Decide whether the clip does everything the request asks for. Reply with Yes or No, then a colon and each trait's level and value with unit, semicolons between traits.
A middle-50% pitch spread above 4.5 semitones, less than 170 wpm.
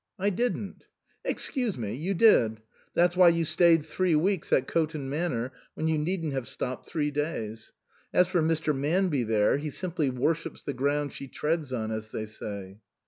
No: average, 5.2 semitones; average, 185 wpm